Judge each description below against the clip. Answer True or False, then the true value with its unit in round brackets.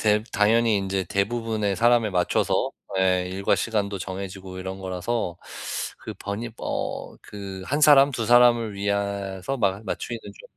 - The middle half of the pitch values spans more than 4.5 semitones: False (3.4 semitones)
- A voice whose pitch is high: False (100 Hz)